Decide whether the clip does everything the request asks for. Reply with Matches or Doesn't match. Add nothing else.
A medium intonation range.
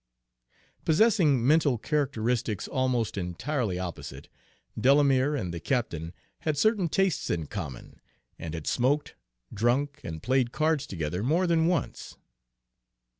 Doesn't match